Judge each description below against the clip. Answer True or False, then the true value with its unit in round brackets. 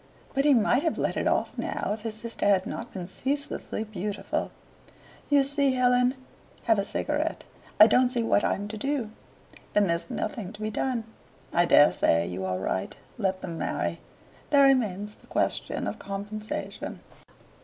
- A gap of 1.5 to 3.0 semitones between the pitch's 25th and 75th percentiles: False (4.8 semitones)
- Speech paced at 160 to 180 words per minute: True (170 wpm)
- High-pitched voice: True (215 Hz)